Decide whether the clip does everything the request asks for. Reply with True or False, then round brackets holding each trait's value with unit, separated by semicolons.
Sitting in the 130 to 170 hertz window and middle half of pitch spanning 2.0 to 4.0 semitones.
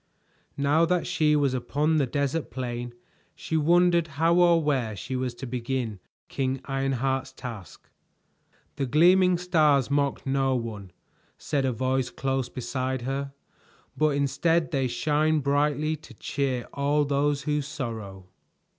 True (140 Hz; 2.9 semitones)